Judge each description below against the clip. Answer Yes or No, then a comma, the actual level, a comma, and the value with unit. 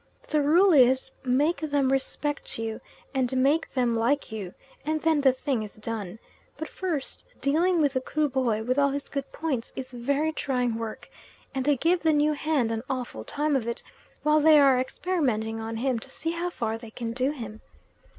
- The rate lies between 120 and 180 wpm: No, average, 190 wpm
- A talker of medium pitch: No, very high, 270 Hz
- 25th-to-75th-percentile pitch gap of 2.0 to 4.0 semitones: No, average, 4.4 semitones